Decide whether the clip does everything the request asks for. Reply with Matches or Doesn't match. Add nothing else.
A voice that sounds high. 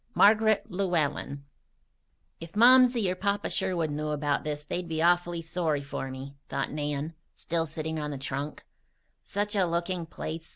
Doesn't match